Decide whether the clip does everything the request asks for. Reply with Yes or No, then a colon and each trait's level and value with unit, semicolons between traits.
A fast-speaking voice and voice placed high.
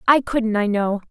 Yes: fast, 215 wpm; high, 225 Hz